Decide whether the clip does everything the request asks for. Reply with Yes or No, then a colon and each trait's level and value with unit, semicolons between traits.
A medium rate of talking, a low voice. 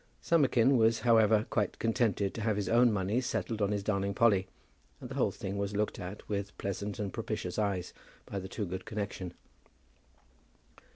Yes: average, 170 wpm; low, 105 Hz